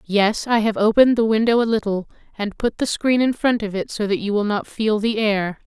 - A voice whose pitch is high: Yes, high, 215 Hz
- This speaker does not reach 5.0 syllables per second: No, 5.4 syllables/s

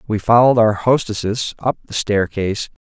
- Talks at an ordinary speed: Yes, average, 145 wpm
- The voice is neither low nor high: No, low, 110 Hz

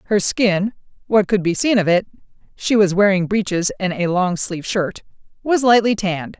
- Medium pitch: No, high, 195 Hz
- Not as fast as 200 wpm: Yes, average, 170 wpm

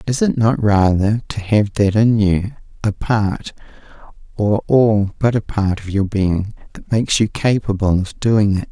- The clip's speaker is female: No, male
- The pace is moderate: Yes, average, 180 wpm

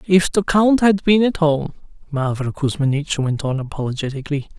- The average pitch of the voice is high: No, medium, 155 Hz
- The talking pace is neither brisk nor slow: Yes, average, 155 wpm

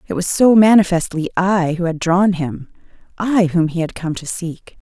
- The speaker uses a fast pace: No, average, 195 wpm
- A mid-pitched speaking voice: Yes, medium, 180 Hz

